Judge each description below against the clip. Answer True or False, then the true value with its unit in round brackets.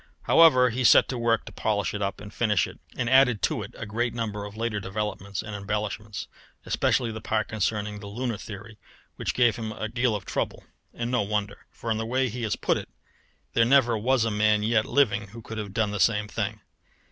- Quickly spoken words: True (220 wpm)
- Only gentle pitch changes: True (2.2 semitones)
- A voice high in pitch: False (110 Hz)